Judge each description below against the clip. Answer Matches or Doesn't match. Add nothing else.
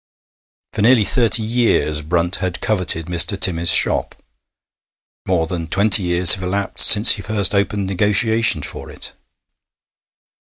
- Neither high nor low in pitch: Doesn't match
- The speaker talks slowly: Matches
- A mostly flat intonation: Doesn't match